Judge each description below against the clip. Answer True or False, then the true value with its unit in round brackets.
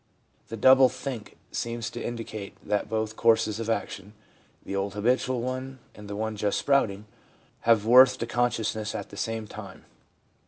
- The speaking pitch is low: True (115 Hz)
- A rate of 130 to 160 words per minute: False (185 wpm)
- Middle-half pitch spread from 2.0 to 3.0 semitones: True (2.7 semitones)